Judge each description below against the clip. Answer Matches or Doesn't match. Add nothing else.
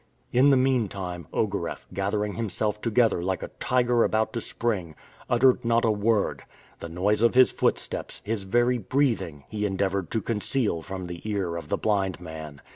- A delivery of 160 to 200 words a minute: Matches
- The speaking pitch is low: Matches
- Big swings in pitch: Doesn't match